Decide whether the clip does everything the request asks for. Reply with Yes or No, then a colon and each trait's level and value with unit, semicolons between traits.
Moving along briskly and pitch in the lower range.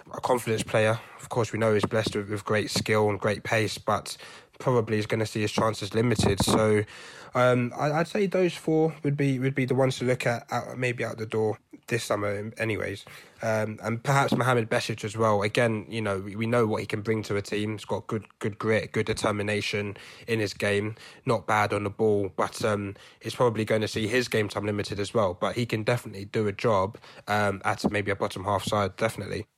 Yes: fast, 220 wpm; low, 110 Hz